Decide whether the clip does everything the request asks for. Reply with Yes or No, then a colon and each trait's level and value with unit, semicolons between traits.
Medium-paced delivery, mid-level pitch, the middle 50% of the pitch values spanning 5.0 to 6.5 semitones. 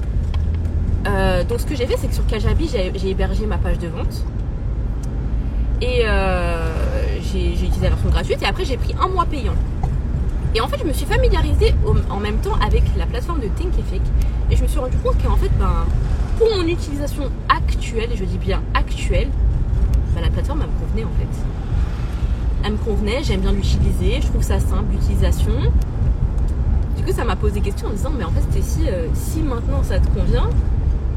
No: average, 205 wpm; very low, 75 Hz; wide, 5.4 semitones